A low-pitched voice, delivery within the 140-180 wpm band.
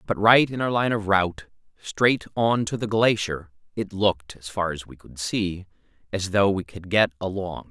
No: low, 100 Hz; average, 200 wpm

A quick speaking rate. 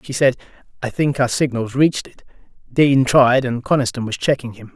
No: average, 190 wpm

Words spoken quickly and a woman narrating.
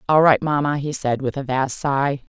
Yes: fast, 230 wpm; female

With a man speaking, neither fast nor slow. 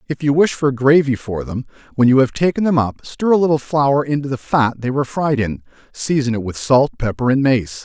No: male; fast, 235 wpm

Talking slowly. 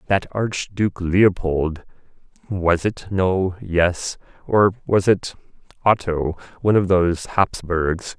Yes: slow, 110 wpm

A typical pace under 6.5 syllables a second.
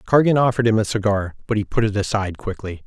No: 6.8 syllables/s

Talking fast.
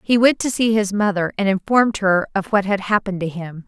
Yes: fast, 245 wpm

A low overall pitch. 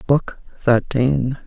Yes: low, 130 Hz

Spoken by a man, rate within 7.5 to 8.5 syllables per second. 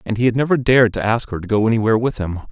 Yes: male; 7.7 syllables/s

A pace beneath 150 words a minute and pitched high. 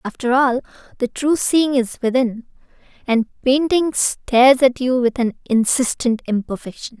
Yes: slow, 135 wpm; very high, 250 Hz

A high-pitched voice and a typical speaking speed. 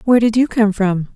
No: high, 215 Hz; fast, 260 wpm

